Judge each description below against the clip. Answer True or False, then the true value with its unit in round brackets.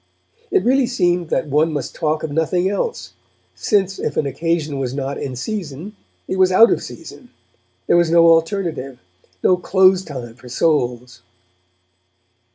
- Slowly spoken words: False (155 wpm)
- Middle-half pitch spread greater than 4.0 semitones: True (5.2 semitones)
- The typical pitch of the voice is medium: True (165 Hz)